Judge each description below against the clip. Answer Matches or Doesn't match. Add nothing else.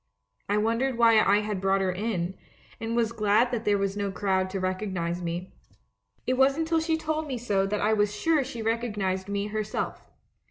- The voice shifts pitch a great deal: Doesn't match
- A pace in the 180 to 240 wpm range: Matches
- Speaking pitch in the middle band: Doesn't match